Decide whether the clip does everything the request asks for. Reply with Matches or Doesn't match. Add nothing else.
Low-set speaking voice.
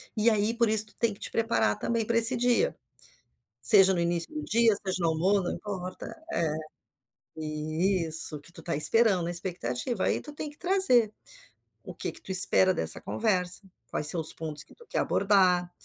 Doesn't match